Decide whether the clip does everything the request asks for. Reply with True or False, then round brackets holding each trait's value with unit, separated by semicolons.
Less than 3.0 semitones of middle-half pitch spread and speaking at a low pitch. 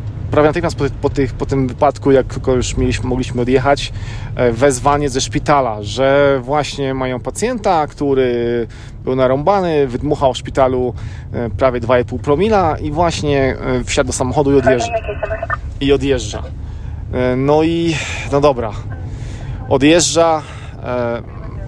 False (3.3 semitones; 130 Hz)